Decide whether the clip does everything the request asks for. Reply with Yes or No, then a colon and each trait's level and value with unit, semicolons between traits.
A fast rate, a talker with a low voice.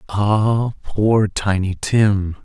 No: slow, 100 wpm; low, 105 Hz